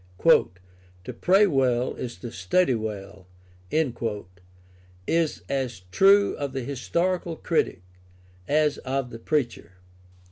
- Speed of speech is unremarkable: No, slow, 105 wpm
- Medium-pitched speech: No, low, 125 Hz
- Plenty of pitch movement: Yes, wide, 8.7 semitones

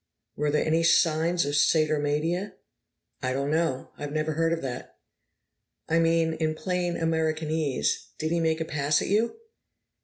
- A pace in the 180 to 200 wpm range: No, average, 155 wpm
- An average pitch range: No, narrow, 1.7 semitones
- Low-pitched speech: No, medium, 160 Hz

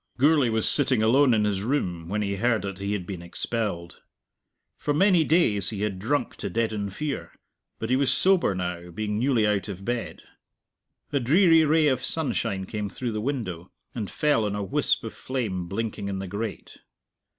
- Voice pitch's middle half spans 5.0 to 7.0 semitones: Yes, wide, 5.4 semitones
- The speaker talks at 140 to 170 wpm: No, average, 185 wpm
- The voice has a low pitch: Yes, low, 110 Hz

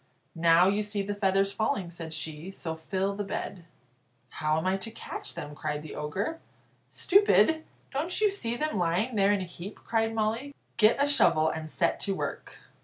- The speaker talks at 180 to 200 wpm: Yes, average, 185 wpm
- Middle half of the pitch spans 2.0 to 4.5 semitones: No, average, 5.0 semitones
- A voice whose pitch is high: Yes, high, 195 Hz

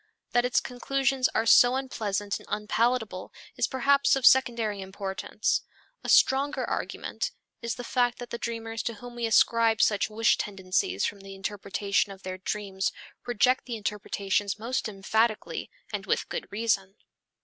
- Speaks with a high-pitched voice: Yes, high, 225 Hz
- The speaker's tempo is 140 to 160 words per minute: Yes, average, 150 wpm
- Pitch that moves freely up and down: No, average, 3.5 semitones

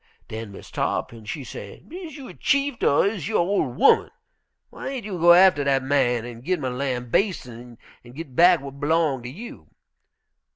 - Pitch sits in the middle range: Yes, medium, 145 Hz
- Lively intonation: Yes, wide, 7.2 semitones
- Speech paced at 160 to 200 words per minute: Yes, average, 190 wpm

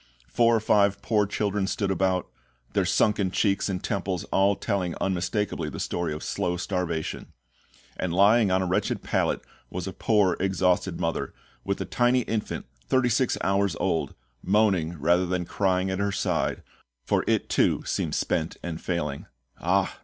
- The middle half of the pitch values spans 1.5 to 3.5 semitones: Yes, narrow, 2.5 semitones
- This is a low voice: Yes, very low, 95 Hz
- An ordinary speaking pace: Yes, average, 160 wpm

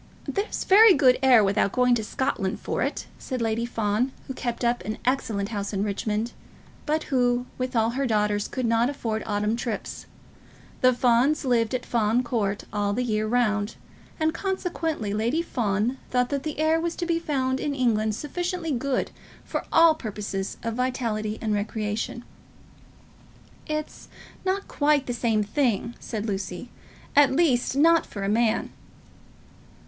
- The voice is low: No, high, 240 Hz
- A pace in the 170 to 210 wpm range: No, average, 155 wpm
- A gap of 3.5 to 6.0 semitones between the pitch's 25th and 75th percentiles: Yes, average, 4.5 semitones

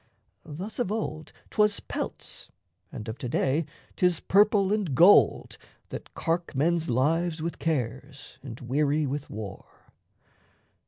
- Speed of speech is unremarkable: No, slow, 125 wpm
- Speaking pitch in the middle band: Yes, medium, 155 Hz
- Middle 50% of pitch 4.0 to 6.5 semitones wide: Yes, average, 5.1 semitones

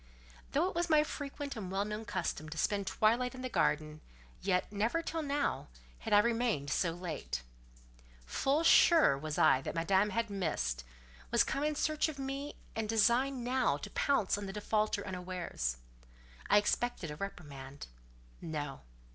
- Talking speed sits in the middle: Yes, average, 160 wpm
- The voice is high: Yes, high, 205 Hz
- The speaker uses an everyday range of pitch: No, wide, 8.8 semitones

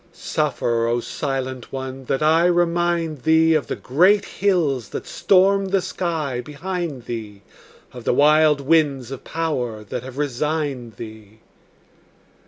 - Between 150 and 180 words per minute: No, slow, 135 wpm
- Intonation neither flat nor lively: Yes, average, 4.9 semitones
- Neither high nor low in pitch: Yes, medium, 145 Hz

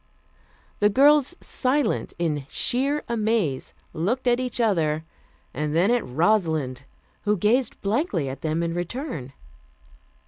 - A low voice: No, high, 205 Hz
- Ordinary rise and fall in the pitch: No, wide, 7.8 semitones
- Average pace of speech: No, slow, 125 wpm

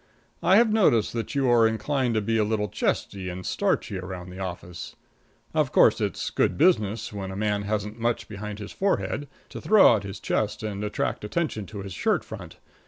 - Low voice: Yes, low, 105 Hz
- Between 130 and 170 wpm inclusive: No, average, 195 wpm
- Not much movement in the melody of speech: No, average, 3.2 semitones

